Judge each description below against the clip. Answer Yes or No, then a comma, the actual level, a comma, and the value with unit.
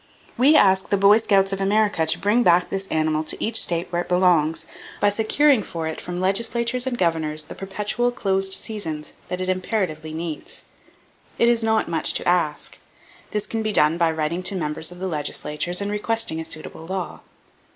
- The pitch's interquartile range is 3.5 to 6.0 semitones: Yes, average, 4.5 semitones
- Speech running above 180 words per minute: Yes, average, 190 wpm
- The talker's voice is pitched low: No, medium, 185 Hz